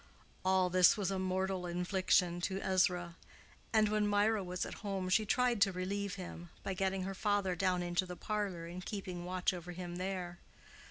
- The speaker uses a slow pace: No, average, 180 wpm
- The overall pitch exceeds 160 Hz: Yes, medium, 185 Hz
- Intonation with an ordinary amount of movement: No, narrow, 1.8 semitones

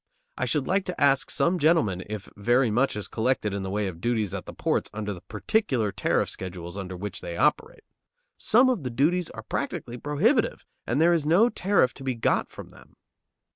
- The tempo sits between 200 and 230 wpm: Yes, fast, 205 wpm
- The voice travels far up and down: Yes, wide, 8.3 semitones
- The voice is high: No, low, 125 Hz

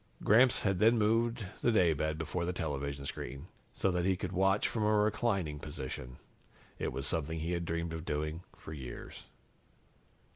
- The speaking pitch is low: Yes, very low, 85 Hz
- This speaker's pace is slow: No, average, 160 wpm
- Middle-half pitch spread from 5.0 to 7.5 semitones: Yes, average, 5.3 semitones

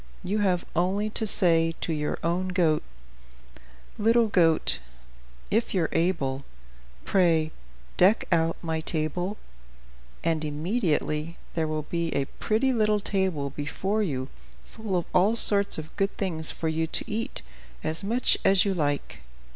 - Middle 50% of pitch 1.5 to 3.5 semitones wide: No, average, 4.2 semitones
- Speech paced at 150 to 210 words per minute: No, average, 140 wpm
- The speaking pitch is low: No, medium, 175 Hz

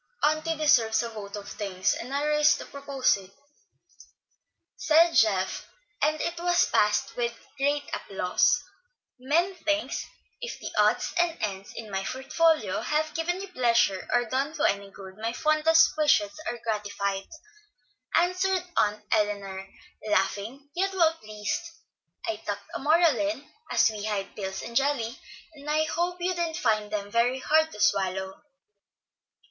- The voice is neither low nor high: No, very high, 255 Hz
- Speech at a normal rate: Yes, average, 150 wpm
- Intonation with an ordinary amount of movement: No, wide, 7.1 semitones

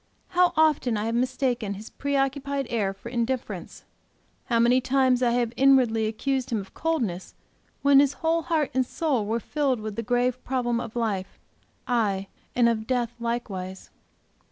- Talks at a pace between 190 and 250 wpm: No, average, 160 wpm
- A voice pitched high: Yes, high, 245 Hz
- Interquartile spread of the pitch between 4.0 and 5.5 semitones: No, average, 3.4 semitones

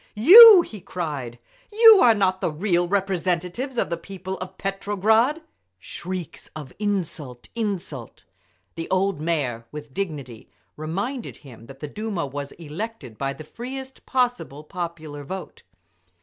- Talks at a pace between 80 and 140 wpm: Yes, slow, 135 wpm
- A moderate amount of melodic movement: No, wide, 6.2 semitones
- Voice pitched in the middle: Yes, medium, 180 Hz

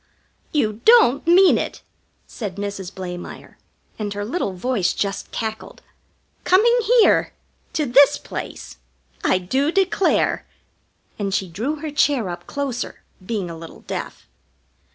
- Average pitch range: No, wide, 7.4 semitones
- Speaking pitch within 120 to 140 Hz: No, high, 220 Hz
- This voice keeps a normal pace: No, slow, 130 wpm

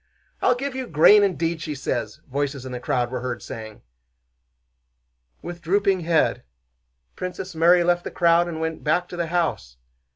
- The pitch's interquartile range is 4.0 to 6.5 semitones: Yes, average, 4.3 semitones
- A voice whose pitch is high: No, medium, 165 Hz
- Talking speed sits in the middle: Yes, average, 165 wpm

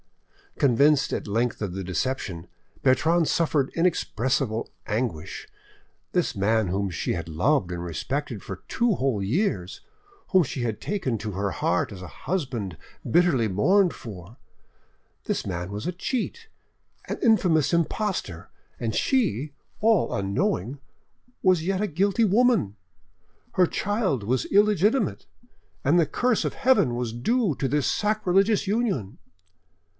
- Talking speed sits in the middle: No, slow, 130 wpm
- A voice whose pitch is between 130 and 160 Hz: Yes, low, 135 Hz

